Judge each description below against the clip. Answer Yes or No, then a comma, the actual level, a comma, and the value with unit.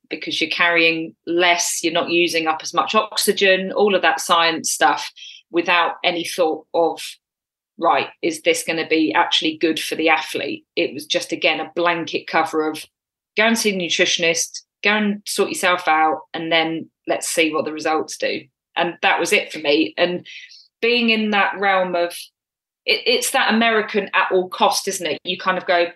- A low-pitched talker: No, medium, 175 Hz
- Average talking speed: Yes, average, 190 wpm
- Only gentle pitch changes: No, average, 3.4 semitones